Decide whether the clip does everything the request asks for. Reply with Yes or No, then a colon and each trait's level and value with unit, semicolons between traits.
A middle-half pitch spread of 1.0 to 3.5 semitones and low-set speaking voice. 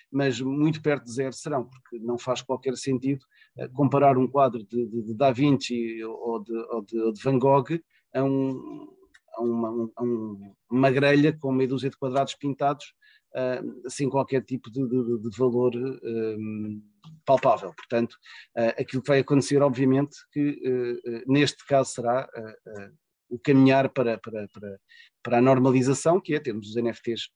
Yes: average, 2.8 semitones; low, 130 Hz